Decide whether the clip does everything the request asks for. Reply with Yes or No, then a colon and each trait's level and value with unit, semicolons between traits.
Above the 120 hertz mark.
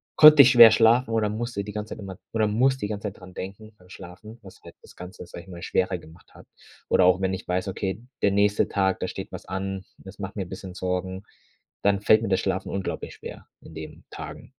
No: very low, 95 Hz